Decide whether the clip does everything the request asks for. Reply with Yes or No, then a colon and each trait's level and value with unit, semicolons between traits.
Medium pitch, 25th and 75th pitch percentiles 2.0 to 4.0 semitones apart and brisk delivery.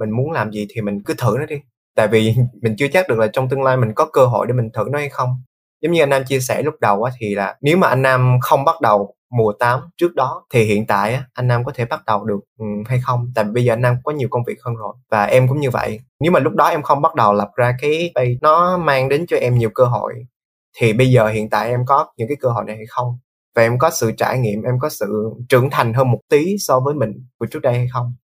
No: low, 125 Hz; average, 3.7 semitones; fast, 290 wpm